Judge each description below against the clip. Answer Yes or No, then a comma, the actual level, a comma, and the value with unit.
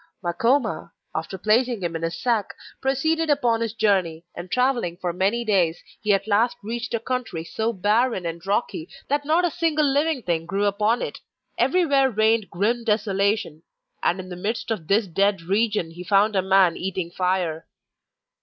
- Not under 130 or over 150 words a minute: No, average, 175 wpm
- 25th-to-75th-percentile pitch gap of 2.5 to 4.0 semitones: No, average, 4.8 semitones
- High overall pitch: Yes, high, 210 Hz